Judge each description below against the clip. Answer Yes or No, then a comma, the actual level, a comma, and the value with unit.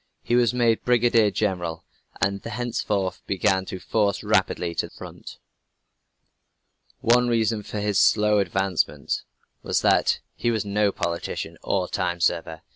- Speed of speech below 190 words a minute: Yes, slow, 135 wpm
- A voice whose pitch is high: No, low, 105 Hz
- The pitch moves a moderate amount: Yes, average, 3.5 semitones